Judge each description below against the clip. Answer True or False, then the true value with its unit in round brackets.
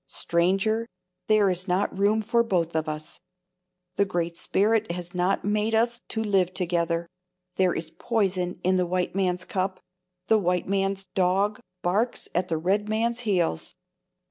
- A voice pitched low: False (190 Hz)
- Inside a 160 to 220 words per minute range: False (150 wpm)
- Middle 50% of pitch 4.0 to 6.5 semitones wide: False (3.0 semitones)